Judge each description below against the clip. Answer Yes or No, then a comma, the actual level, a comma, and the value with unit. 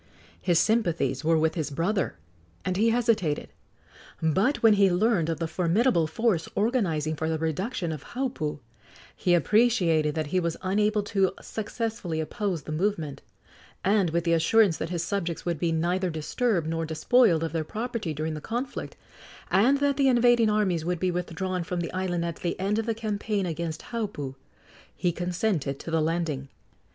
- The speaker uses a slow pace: No, average, 170 wpm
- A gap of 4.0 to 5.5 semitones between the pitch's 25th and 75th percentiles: Yes, average, 4.9 semitones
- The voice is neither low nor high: Yes, medium, 180 Hz